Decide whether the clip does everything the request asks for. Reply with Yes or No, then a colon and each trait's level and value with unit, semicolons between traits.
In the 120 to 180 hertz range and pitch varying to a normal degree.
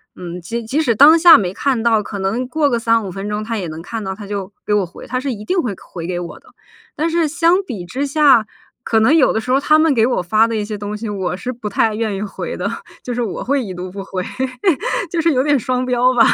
No: high, 225 Hz; average, 4.8 semitones